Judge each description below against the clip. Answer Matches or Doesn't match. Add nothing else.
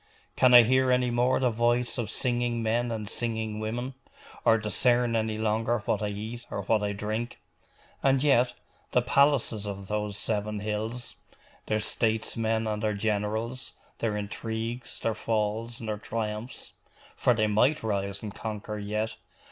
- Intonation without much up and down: Matches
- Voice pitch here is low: Matches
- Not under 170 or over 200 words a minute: Doesn't match